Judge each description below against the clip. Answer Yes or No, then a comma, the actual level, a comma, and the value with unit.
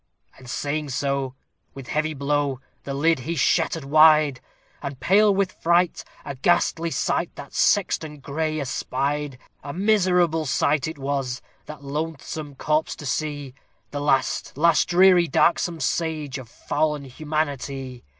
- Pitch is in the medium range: Yes, medium, 150 Hz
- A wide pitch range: No, average, 2.9 semitones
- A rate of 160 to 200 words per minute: No, slow, 135 wpm